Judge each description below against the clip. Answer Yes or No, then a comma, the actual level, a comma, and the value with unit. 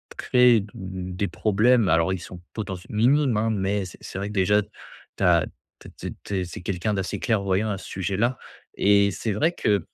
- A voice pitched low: Yes, low, 100 Hz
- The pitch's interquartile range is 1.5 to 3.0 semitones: Yes, narrow, 2.6 semitones